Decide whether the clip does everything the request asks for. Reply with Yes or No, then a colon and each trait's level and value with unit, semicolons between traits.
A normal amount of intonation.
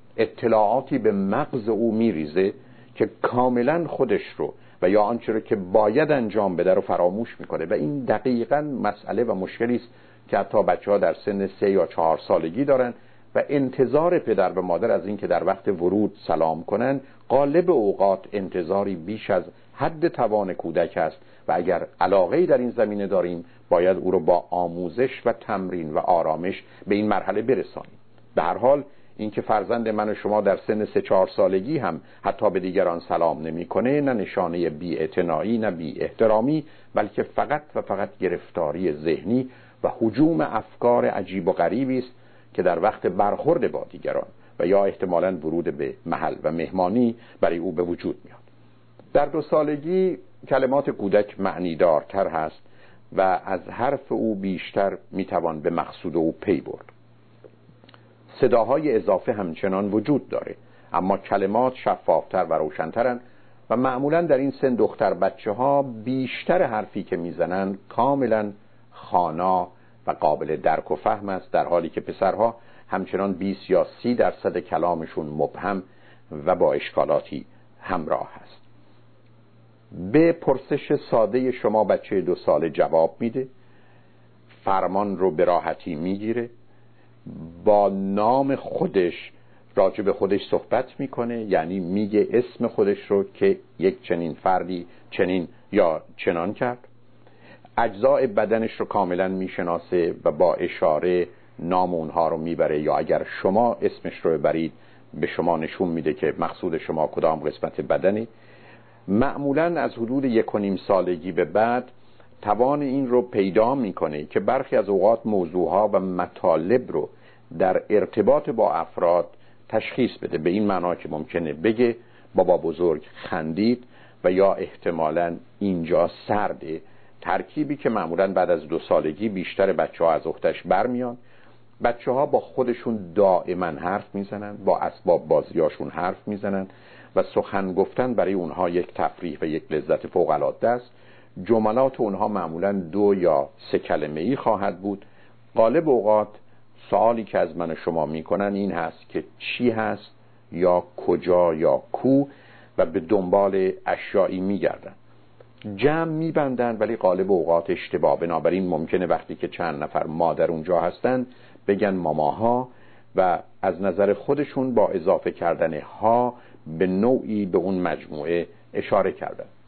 Yes: average, 4.9 semitones